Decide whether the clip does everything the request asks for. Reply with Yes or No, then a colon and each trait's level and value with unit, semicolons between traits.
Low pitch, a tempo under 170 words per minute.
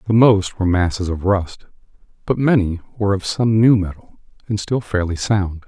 No: low, 100 Hz; average, 180 wpm